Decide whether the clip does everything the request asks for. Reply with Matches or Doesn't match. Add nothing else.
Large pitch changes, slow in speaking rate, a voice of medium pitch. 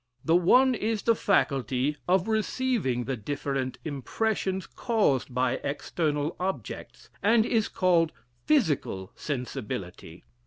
Matches